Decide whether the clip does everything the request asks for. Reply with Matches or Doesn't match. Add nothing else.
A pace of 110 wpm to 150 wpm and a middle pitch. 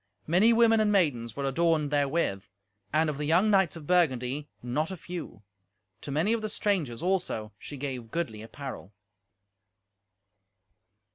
Matches